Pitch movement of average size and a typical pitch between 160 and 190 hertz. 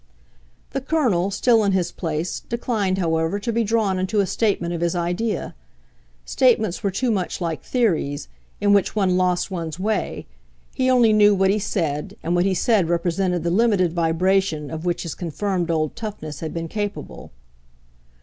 Yes: average, 3.8 semitones; medium, 185 Hz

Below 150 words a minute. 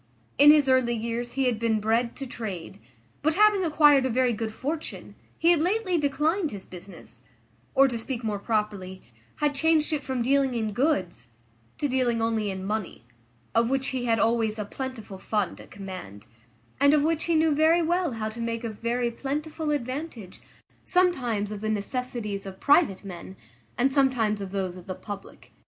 No: average, 180 wpm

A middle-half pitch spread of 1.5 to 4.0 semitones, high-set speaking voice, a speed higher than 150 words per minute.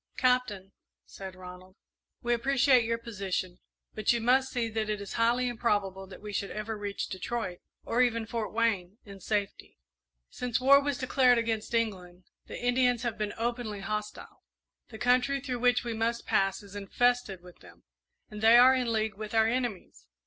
Yes: average, 3.4 semitones; high, 225 Hz; average, 175 wpm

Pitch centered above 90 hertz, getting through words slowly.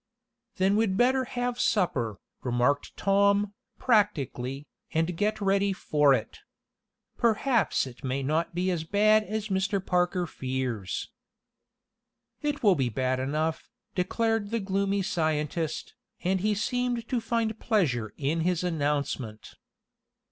Yes: medium, 185 Hz; slow, 125 wpm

